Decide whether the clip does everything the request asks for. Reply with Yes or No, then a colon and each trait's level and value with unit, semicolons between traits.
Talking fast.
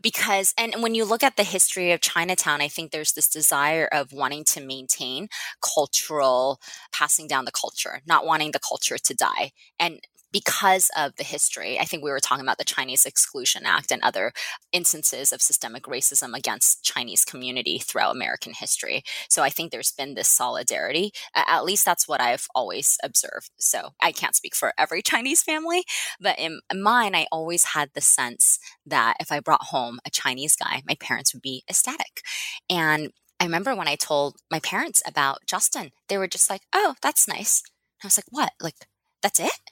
No: average, 190 wpm